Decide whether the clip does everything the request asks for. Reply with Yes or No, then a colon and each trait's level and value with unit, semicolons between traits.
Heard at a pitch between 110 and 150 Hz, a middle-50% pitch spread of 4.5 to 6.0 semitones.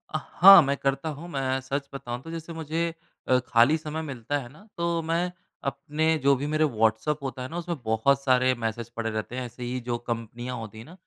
Yes: low, 135 Hz; average, 4.8 semitones